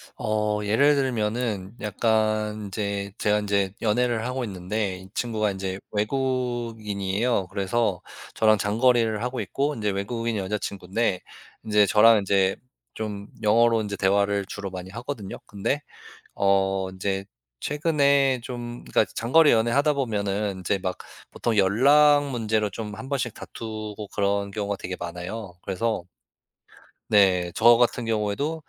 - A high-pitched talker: No, low, 105 Hz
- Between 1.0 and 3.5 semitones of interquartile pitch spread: Yes, average, 3.2 semitones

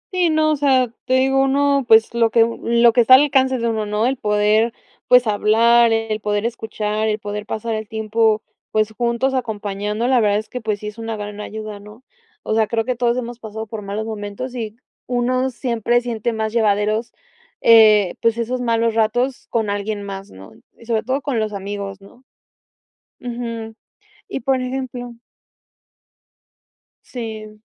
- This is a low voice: No, high, 225 Hz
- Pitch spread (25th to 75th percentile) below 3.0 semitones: Yes, narrow, 2.4 semitones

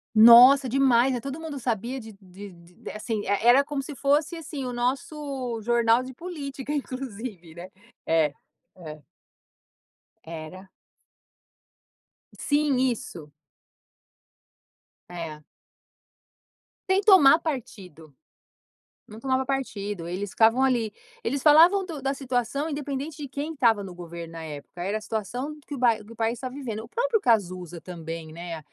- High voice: Yes, high, 240 Hz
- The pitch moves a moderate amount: No, wide, 6.8 semitones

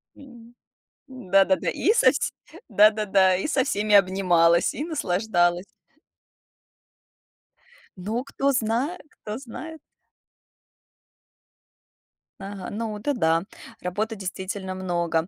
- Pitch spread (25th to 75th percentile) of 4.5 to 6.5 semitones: Yes, average, 4.9 semitones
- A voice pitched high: Yes, high, 210 Hz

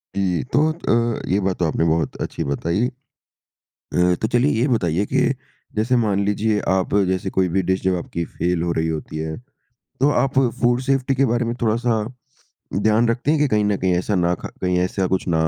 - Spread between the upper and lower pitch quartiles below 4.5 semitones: No, average, 5.1 semitones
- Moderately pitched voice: No, low, 100 Hz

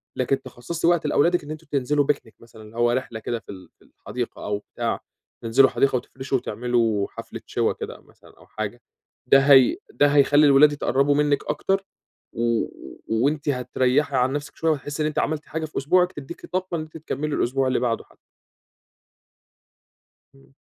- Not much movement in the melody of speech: No, average, 3.5 semitones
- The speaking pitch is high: No, low, 135 Hz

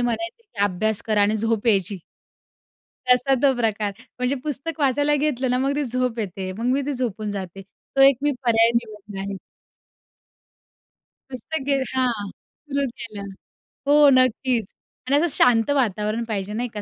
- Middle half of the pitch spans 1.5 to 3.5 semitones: No, average, 4.4 semitones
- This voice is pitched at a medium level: No, high, 235 Hz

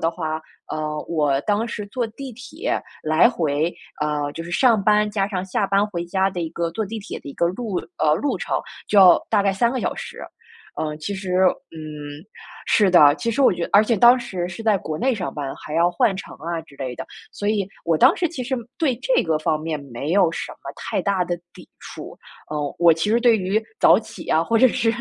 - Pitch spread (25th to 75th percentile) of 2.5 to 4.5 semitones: No, average, 5.3 semitones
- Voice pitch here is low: No, medium, 185 Hz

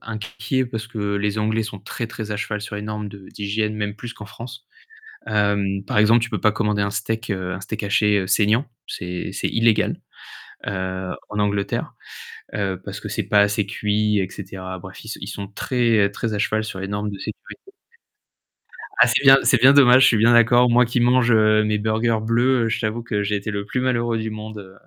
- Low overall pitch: Yes, low, 105 Hz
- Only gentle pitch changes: Yes, narrow, 2.1 semitones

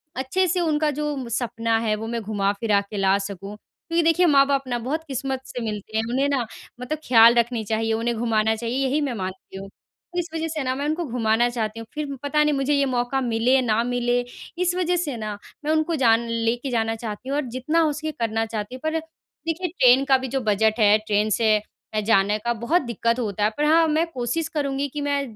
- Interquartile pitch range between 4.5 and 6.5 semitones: Yes, average, 4.9 semitones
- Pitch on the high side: Yes, high, 245 Hz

